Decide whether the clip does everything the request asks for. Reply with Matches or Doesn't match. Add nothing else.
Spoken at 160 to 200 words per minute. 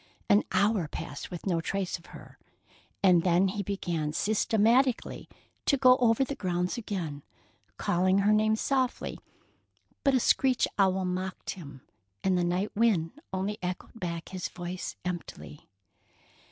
Doesn't match